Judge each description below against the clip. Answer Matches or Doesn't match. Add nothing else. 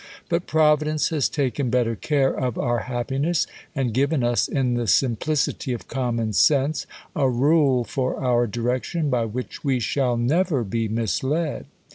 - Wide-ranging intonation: Doesn't match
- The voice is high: Doesn't match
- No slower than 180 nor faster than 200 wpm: Doesn't match